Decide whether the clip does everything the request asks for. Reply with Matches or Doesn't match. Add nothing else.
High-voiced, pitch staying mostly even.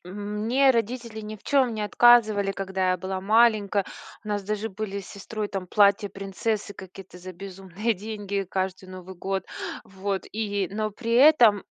Matches